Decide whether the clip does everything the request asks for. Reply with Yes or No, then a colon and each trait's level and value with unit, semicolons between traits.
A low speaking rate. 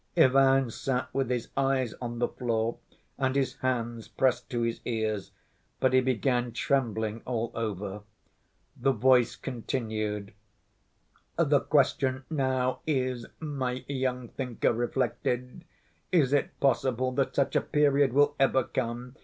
Yes: slow, 130 wpm